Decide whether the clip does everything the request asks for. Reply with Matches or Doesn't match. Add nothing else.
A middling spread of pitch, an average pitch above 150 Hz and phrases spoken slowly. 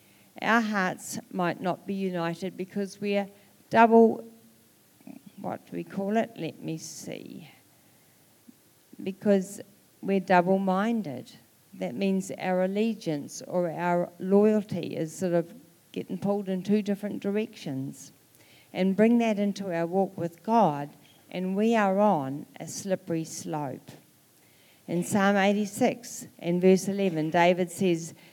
Matches